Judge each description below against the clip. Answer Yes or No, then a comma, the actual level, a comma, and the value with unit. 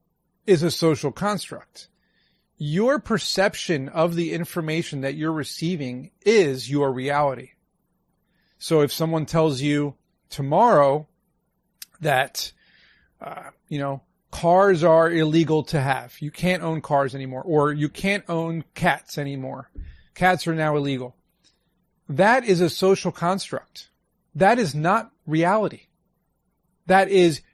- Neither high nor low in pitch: Yes, medium, 165 Hz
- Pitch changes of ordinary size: Yes, average, 3.9 semitones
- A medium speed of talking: No, slow, 120 wpm